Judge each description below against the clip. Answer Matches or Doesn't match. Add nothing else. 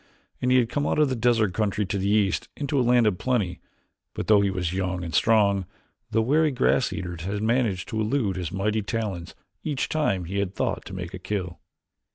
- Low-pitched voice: Matches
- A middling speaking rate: Doesn't match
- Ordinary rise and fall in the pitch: Matches